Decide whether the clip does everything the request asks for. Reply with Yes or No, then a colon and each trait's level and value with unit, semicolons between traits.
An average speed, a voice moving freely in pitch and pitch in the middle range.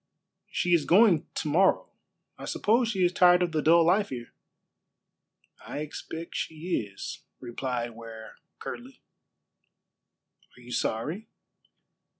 No: slow, 125 wpm; wide, 6.6 semitones; medium, 160 Hz